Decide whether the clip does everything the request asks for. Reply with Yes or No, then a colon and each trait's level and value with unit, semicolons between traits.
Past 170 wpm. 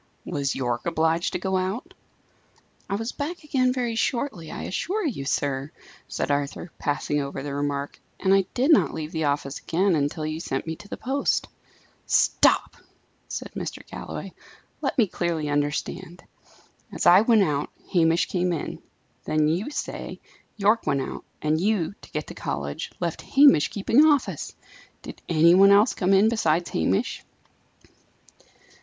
No: average, 160 wpm